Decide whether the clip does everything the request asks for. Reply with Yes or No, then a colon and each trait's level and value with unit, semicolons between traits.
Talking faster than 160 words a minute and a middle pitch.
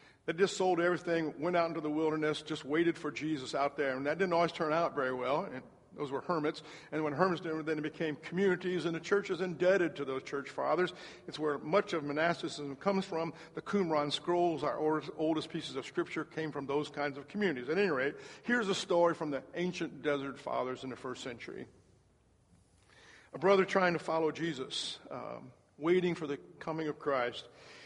Yes: average, 200 wpm; medium, 160 Hz